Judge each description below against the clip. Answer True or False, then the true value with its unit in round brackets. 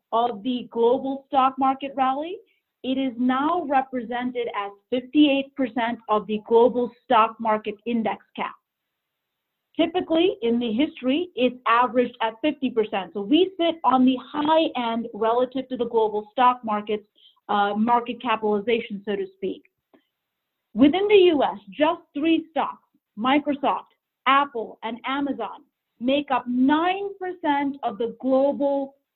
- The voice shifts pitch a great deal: False (3.6 semitones)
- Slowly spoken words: True (130 wpm)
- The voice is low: False (255 Hz)